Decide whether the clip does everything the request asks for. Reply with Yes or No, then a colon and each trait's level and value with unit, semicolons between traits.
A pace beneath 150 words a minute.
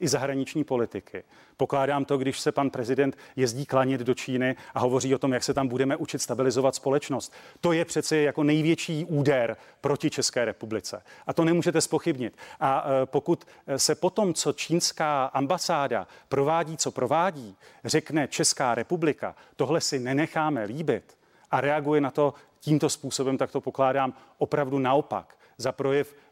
No: average, 155 wpm